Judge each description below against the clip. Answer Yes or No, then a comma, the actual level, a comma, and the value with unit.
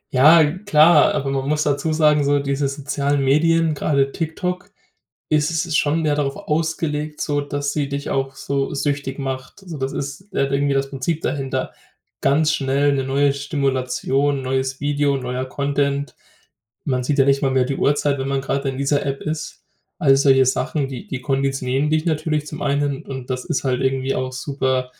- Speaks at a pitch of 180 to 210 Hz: No, medium, 140 Hz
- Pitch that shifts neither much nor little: No, narrow, 1.8 semitones